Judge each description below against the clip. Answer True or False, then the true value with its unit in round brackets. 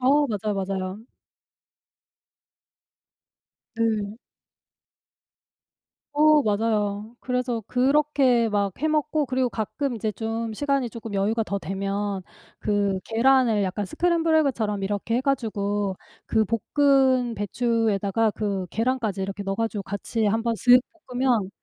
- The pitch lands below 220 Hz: False (225 Hz)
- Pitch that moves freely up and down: False (3.9 semitones)